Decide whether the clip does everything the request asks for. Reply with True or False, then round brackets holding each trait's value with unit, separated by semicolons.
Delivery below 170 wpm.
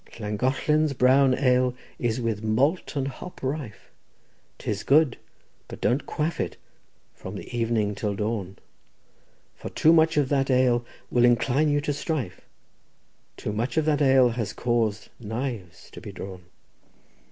True (145 wpm)